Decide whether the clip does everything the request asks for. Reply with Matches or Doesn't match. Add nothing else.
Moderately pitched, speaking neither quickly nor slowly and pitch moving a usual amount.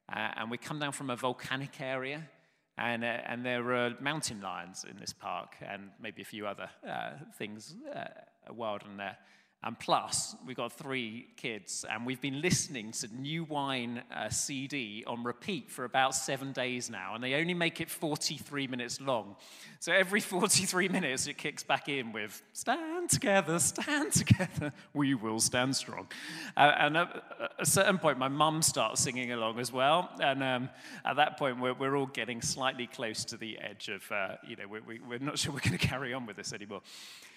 Doesn't match